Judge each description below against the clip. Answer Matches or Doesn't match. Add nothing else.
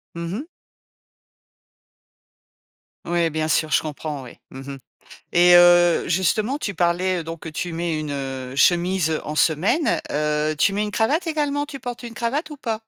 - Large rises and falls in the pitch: Matches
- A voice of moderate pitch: Matches